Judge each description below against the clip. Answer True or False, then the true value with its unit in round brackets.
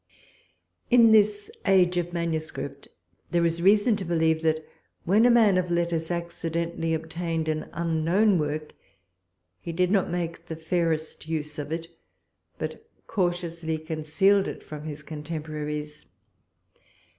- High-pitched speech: False (165 Hz)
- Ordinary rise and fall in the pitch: False (2.2 semitones)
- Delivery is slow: True (130 wpm)